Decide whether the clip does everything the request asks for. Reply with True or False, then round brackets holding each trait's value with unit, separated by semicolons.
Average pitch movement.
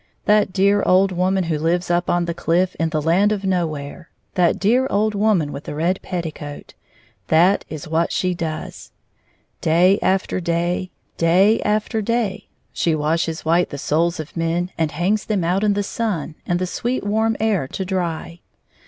True (3.3 semitones)